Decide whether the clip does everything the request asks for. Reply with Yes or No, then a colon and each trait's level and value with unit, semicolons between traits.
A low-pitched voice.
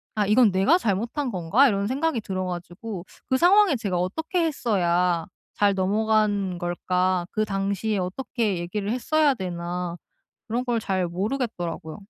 No: high, 200 Hz